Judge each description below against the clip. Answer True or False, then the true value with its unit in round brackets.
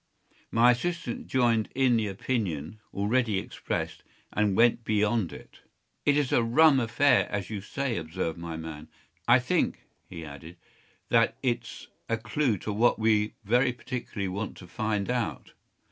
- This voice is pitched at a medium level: False (110 Hz)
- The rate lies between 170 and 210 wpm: False (150 wpm)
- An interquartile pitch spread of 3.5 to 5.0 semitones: True (3.9 semitones)